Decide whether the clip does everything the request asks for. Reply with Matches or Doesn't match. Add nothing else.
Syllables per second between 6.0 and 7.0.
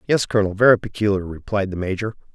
Matches